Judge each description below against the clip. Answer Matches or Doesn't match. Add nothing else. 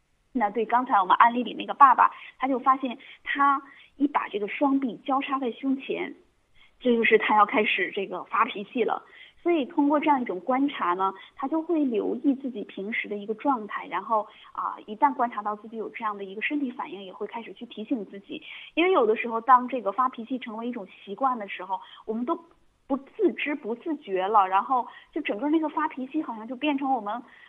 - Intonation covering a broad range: Doesn't match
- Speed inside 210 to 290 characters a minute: Doesn't match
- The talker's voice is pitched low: Doesn't match